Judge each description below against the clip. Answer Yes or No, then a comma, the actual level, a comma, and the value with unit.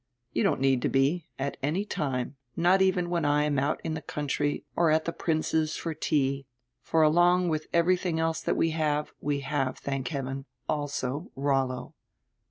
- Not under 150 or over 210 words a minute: Yes, average, 180 wpm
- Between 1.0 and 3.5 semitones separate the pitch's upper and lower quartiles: Yes, average, 3.1 semitones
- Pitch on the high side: No, medium, 150 Hz